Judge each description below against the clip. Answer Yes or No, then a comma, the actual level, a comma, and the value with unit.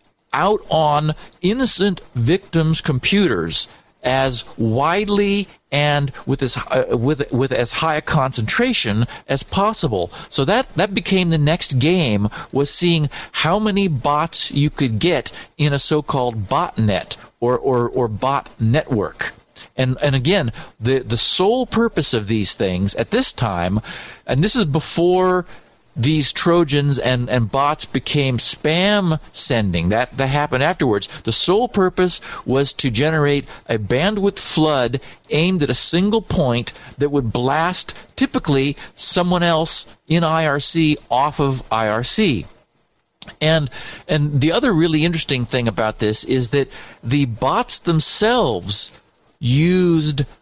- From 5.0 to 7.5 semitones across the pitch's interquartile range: Yes, average, 5.3 semitones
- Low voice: No, medium, 145 Hz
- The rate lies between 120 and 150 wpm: Yes, slow, 135 wpm